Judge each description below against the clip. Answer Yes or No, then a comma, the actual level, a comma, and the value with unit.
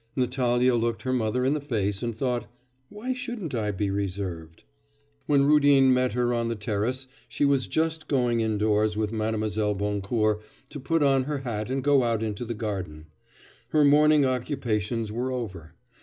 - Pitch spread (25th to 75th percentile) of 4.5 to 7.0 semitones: No, average, 4.1 semitones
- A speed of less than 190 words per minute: Yes, average, 170 wpm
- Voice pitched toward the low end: Yes, low, 120 Hz